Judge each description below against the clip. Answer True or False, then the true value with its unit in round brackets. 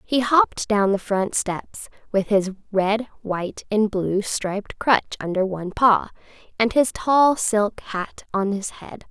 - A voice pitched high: True (210 Hz)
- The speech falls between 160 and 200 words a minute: True (165 wpm)